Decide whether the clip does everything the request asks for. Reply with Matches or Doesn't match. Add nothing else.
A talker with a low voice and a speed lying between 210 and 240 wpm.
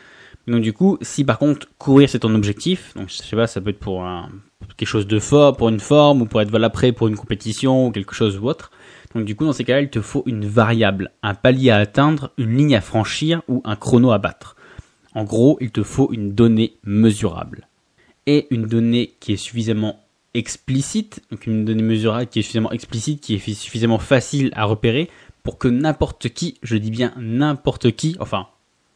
Matches